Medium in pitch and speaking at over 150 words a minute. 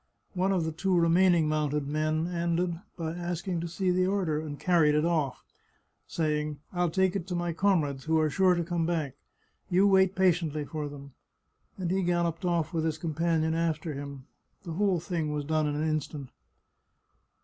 Yes: medium, 165 Hz; average, 185 wpm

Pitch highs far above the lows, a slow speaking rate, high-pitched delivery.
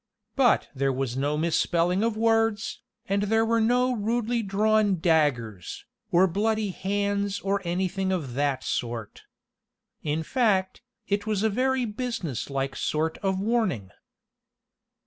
Yes: wide, 6.0 semitones; slow, 130 wpm; high, 195 Hz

